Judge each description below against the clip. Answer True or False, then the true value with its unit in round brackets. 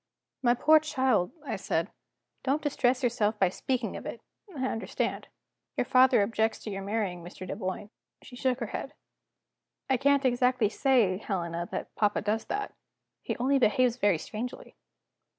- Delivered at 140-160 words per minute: True (155 wpm)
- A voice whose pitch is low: False (235 Hz)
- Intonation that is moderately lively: True (4.4 semitones)